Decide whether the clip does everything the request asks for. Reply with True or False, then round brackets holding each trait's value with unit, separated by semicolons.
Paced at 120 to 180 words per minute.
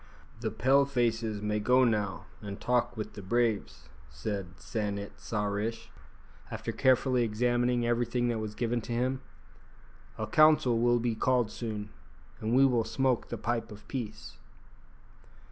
True (150 wpm)